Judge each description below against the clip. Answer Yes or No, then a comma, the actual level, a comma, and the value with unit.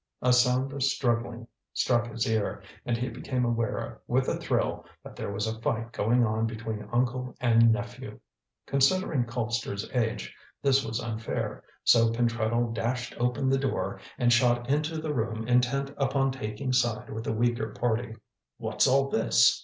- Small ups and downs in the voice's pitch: Yes, narrow, 2.1 semitones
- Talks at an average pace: Yes, average, 160 wpm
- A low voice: Yes, low, 120 Hz